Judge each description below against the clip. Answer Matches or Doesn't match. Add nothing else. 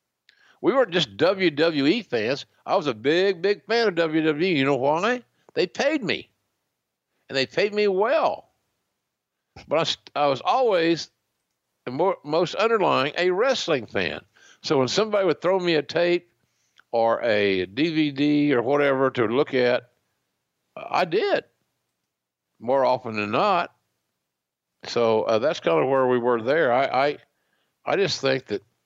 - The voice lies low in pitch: Doesn't match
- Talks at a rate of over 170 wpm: Doesn't match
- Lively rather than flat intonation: Matches